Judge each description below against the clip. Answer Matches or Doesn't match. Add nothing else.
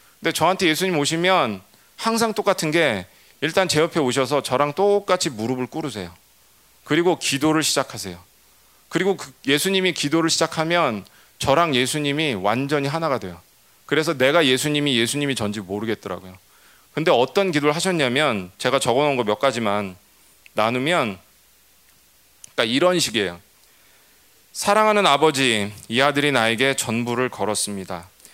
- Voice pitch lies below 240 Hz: Matches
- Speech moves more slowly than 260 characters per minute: Doesn't match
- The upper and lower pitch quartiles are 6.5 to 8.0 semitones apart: Matches